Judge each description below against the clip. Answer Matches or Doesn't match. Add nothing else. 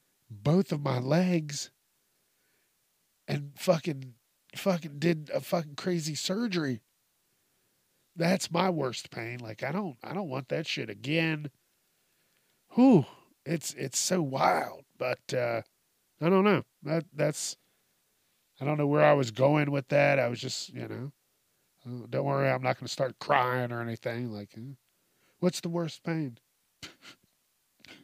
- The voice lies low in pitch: Doesn't match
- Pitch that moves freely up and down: Doesn't match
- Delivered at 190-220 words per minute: Doesn't match